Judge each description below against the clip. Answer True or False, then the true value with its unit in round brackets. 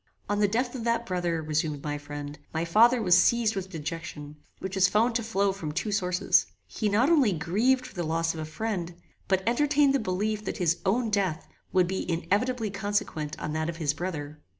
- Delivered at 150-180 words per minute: False (205 wpm)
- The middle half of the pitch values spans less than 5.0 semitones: False (5.4 semitones)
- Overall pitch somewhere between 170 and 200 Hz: True (190 Hz)